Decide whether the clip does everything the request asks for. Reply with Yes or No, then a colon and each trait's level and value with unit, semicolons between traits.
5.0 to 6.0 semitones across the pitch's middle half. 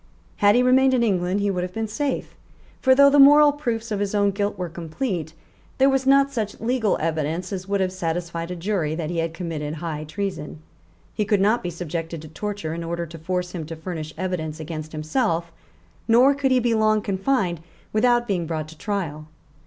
Yes: wide, 5.5 semitones